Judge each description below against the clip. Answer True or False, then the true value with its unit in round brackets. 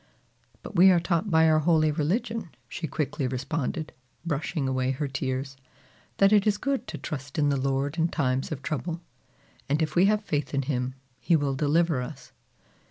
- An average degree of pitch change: True (4.0 semitones)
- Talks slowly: False (180 wpm)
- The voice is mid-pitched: True (155 Hz)